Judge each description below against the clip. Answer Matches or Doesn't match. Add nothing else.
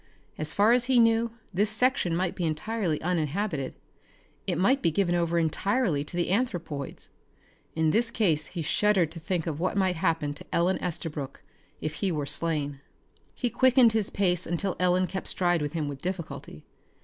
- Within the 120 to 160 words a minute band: Doesn't match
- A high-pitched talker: Doesn't match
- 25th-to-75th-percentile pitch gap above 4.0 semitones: Matches